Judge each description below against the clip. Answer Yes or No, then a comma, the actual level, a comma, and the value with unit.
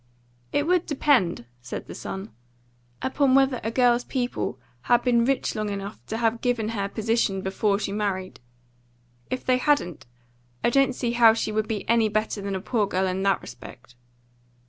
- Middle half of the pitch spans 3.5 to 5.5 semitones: Yes, average, 3.9 semitones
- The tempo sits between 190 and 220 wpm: No, average, 175 wpm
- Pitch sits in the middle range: No, high, 220 Hz